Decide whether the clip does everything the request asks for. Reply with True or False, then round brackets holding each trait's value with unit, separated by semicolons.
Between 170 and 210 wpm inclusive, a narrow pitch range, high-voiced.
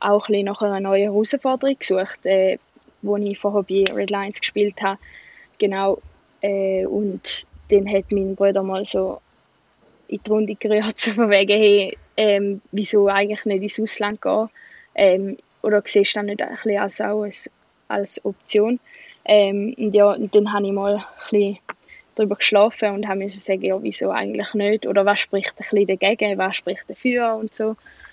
False (160 wpm; 1.3 semitones; 205 Hz)